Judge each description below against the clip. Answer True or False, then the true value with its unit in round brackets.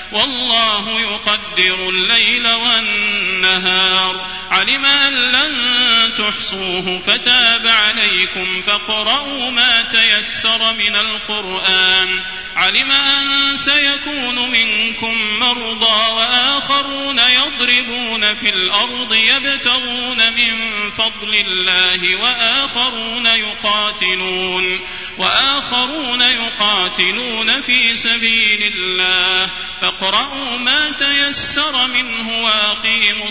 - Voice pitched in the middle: False (225 Hz)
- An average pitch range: True (3.3 semitones)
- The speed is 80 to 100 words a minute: False (70 wpm)